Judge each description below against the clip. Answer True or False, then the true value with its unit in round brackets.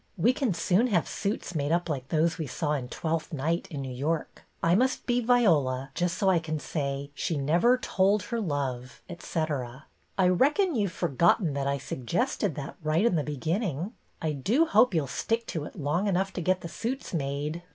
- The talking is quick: True (215 wpm)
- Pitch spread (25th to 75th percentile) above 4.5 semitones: True (5.6 semitones)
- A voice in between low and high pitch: True (165 Hz)